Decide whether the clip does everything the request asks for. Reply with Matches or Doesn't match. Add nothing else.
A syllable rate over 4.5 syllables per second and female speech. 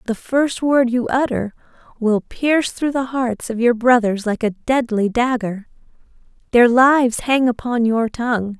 Doesn't match